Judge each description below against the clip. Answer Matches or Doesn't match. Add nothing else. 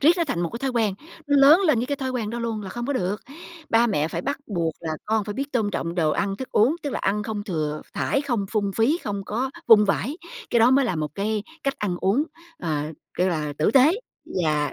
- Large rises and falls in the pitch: Matches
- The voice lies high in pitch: Matches